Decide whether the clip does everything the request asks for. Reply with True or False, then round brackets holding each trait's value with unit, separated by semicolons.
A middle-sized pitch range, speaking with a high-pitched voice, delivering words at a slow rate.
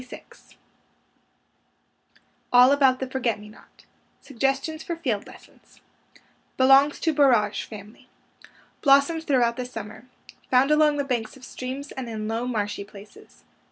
True (3.8 semitones; 255 Hz; 130 wpm)